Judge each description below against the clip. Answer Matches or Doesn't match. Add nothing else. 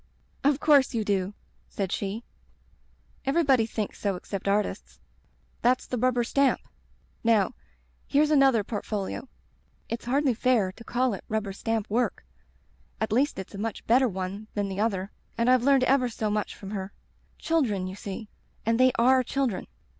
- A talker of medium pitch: Doesn't match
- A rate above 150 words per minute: Matches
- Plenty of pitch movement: Doesn't match